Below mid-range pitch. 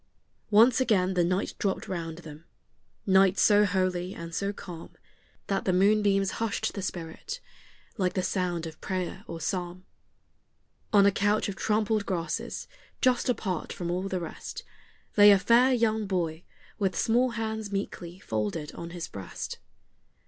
No: high, 190 Hz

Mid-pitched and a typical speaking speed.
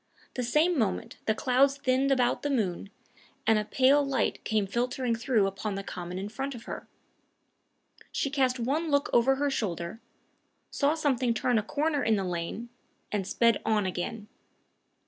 No: high, 240 Hz; average, 165 wpm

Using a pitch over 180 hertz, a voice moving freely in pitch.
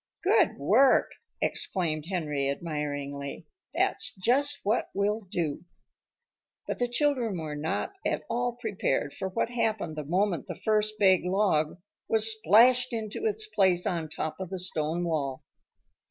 Yes: high, 190 Hz; wide, 6.5 semitones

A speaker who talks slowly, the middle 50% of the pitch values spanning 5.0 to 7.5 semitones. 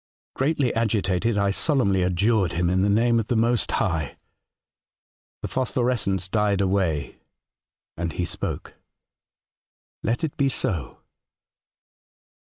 No: slow, 125 wpm; average, 4.5 semitones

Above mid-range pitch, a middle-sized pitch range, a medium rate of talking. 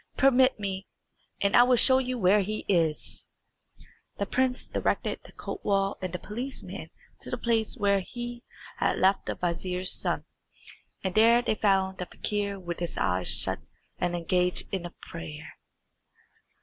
Yes: high, 200 Hz; average, 4.7 semitones; average, 150 wpm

